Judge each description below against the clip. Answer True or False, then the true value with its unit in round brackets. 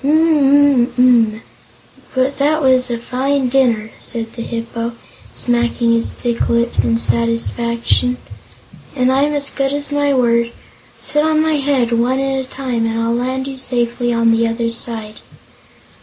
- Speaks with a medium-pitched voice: False (245 Hz)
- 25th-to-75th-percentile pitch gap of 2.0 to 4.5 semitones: True (2.7 semitones)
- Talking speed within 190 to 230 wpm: False (165 wpm)